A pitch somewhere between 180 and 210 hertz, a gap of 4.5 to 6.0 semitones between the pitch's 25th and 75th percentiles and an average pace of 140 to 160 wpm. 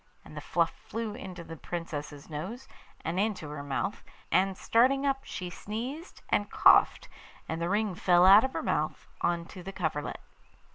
No: medium, 185 Hz; average, 4.9 semitones; average, 175 wpm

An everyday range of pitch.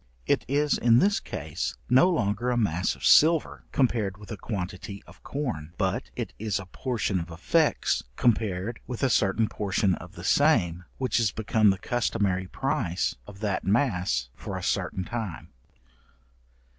Yes: average, 4.7 semitones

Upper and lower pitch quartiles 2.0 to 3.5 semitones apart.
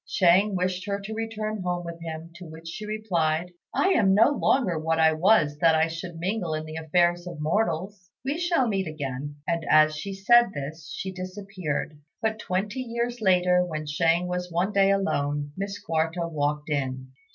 No: average, 4.0 semitones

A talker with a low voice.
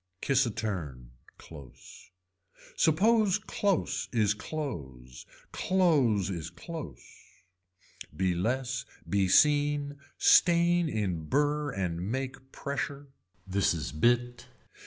Yes: low, 120 Hz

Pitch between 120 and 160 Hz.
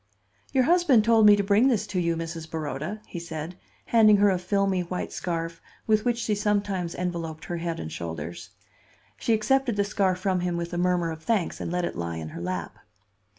No: medium, 180 Hz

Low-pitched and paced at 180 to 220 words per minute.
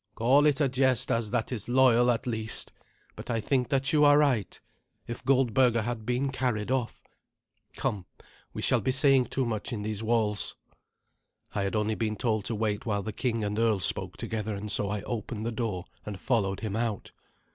Yes: low, 115 Hz; average, 195 wpm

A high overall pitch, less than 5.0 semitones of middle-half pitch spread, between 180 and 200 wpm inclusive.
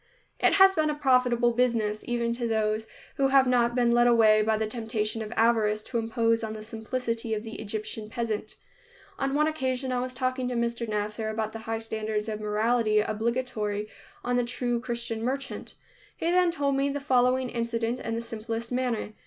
Yes: high, 235 Hz; narrow, 2.4 semitones; average, 190 wpm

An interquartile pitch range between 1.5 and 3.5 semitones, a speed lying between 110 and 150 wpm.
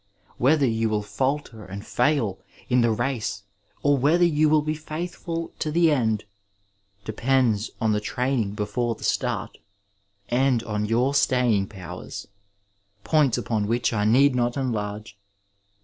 No: average, 4.8 semitones; average, 140 wpm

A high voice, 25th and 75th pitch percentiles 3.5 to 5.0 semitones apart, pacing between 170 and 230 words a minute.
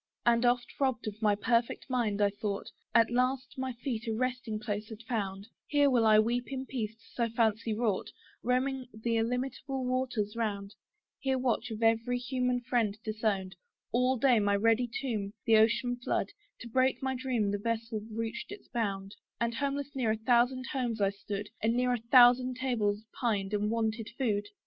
No: high, 230 Hz; average, 2.8 semitones; average, 180 wpm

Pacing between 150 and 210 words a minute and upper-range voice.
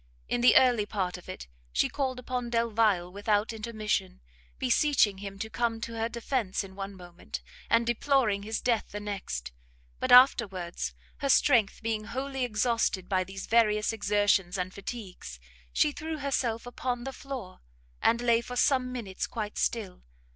Yes: average, 160 wpm; high, 220 Hz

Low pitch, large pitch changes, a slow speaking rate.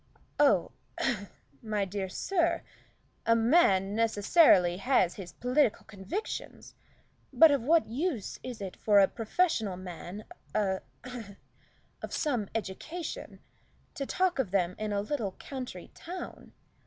No: high, 220 Hz; wide, 6.8 semitones; slow, 125 wpm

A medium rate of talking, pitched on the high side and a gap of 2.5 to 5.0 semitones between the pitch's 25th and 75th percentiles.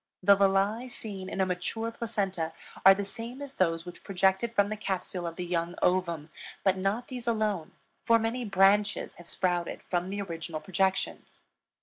Yes: average, 175 wpm; high, 195 Hz; average, 3.2 semitones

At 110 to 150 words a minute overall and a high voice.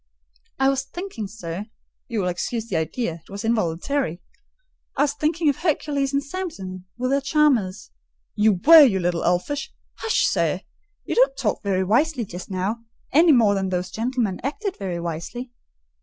No: average, 165 wpm; high, 230 Hz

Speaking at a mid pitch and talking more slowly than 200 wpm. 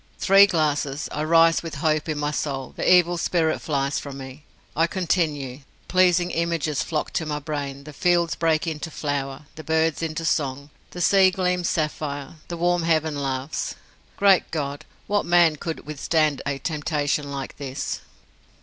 Yes: medium, 155 Hz; average, 160 wpm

